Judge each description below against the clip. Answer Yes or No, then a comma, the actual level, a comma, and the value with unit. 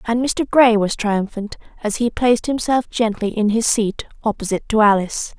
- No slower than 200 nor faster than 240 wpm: No, average, 180 wpm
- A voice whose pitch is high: Yes, high, 225 Hz